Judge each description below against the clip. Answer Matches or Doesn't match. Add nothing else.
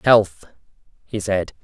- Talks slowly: Matches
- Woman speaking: Doesn't match